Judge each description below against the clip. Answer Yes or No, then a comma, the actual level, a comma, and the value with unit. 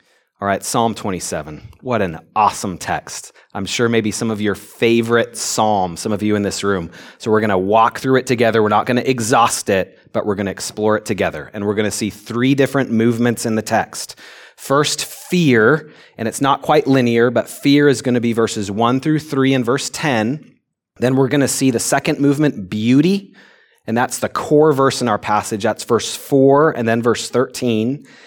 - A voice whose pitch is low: Yes, low, 115 Hz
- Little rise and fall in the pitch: No, average, 3.8 semitones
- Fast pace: Yes, fast, 210 wpm